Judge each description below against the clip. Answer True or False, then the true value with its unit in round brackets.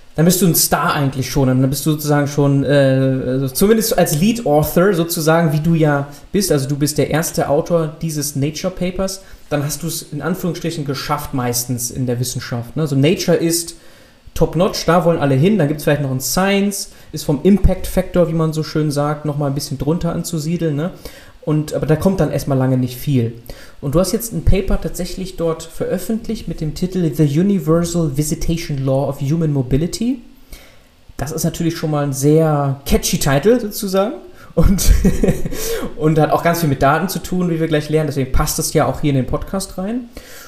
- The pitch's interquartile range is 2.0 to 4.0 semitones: True (3.5 semitones)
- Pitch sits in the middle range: True (160 Hz)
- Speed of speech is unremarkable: False (200 wpm)